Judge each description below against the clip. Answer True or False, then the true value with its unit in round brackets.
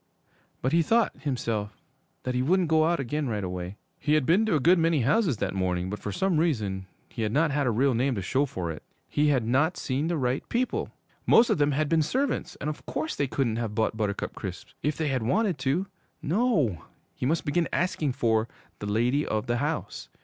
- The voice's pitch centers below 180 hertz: True (140 Hz)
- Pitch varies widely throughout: True (6.1 semitones)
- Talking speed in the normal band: False (220 wpm)